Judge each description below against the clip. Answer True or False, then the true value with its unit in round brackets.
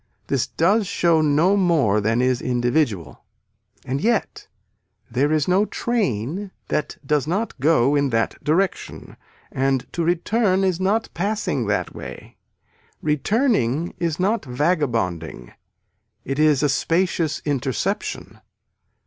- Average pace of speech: False (120 wpm)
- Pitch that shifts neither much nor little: False (6.5 semitones)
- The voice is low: False (155 Hz)